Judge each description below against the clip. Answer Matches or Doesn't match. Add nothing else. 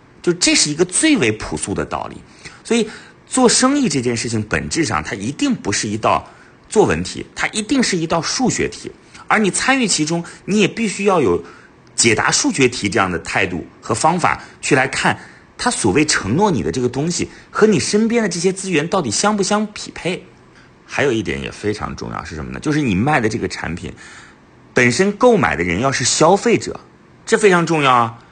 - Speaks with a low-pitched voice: Doesn't match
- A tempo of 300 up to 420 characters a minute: Doesn't match